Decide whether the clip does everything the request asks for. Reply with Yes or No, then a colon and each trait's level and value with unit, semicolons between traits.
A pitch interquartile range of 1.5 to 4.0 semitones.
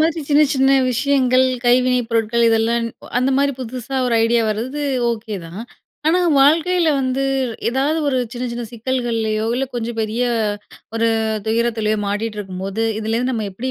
Yes: average, 2.8 semitones